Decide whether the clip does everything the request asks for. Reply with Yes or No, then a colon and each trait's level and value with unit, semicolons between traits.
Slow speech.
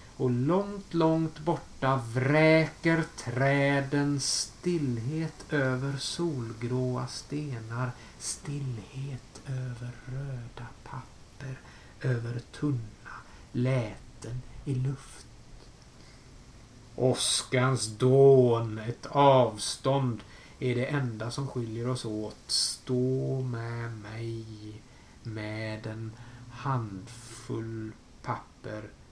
Yes: slow, 75 wpm